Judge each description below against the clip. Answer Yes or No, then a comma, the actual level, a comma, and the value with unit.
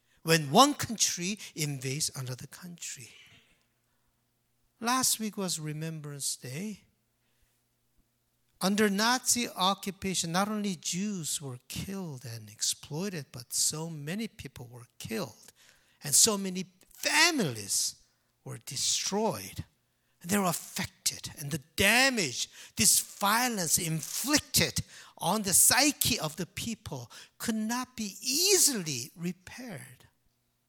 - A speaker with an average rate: No, slow, 105 wpm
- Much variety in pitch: Yes, wide, 7.7 semitones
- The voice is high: No, medium, 165 Hz